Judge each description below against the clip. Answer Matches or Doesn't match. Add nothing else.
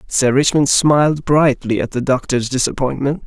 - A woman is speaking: Doesn't match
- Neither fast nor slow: Matches